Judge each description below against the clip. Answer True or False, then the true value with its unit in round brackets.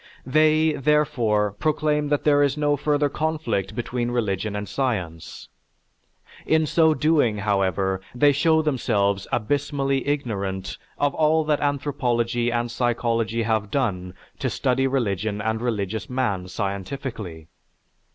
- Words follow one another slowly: True (120 wpm)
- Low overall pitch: True (120 Hz)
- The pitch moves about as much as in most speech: False (6.0 semitones)